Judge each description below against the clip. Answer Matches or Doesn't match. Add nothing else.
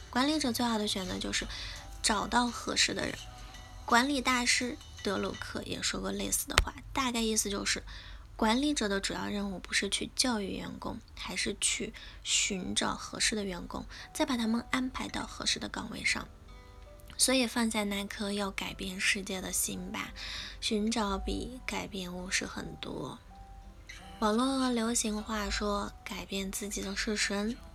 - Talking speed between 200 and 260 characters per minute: Matches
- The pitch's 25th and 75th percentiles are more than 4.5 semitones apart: Doesn't match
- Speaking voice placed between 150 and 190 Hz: Doesn't match